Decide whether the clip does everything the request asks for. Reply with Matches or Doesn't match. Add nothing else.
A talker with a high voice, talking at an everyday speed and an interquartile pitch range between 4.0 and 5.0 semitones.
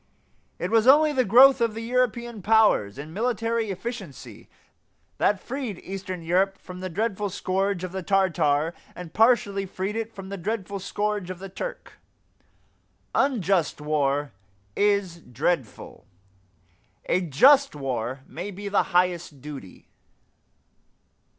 Doesn't match